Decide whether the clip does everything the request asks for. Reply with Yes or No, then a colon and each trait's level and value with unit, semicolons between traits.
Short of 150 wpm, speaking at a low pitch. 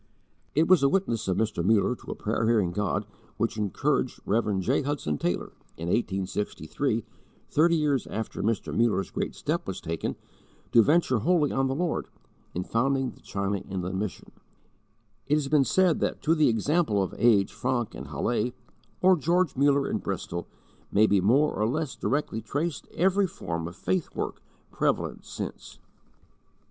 No: average, 165 wpm; low, 115 Hz